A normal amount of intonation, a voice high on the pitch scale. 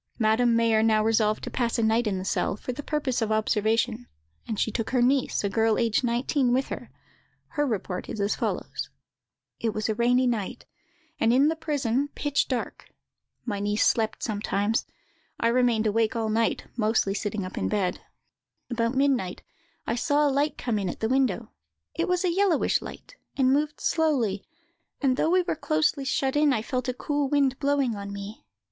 Yes: average, 4.2 semitones; high, 235 Hz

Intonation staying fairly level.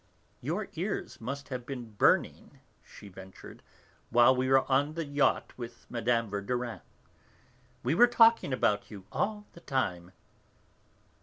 No: average, 4.5 semitones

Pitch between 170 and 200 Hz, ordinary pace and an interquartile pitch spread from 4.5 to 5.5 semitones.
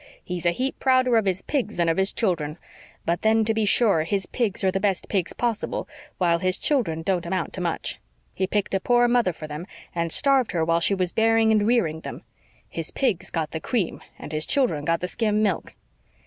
No: high, 190 Hz; fast, 220 wpm; average, 4.9 semitones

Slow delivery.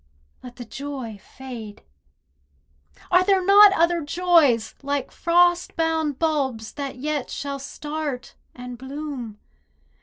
Yes: slow, 115 wpm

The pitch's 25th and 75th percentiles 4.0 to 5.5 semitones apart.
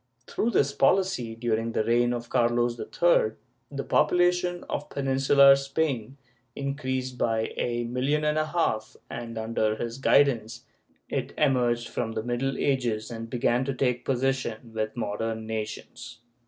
No: average, 3.3 semitones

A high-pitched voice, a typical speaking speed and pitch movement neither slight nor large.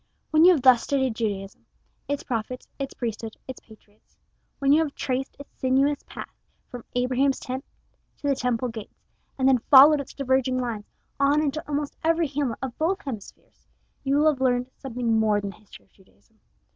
Yes: very high, 260 Hz; average, 185 wpm; average, 3.4 semitones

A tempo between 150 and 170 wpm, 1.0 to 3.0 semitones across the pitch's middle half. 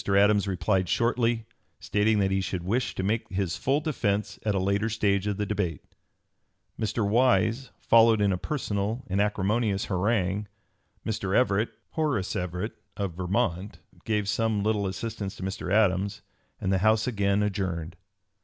No: average, 140 wpm; narrow, 2.4 semitones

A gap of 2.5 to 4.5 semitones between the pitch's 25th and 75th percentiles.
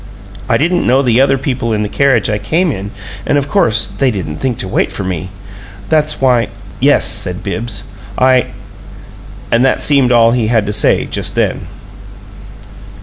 Yes: average, 4.1 semitones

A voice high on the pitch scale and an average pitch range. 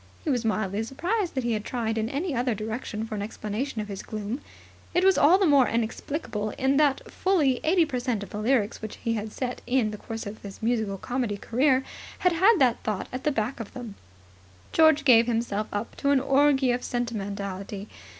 Yes: high, 240 Hz; average, 4.4 semitones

